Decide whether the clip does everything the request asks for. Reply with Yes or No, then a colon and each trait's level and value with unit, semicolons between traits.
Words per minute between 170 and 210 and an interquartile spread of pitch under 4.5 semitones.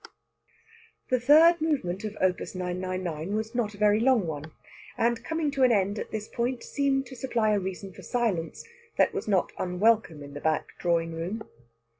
No: average, 180 wpm; average, 5.3 semitones